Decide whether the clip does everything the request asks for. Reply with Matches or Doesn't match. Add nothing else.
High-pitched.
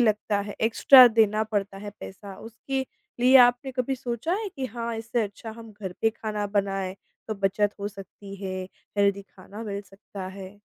Matches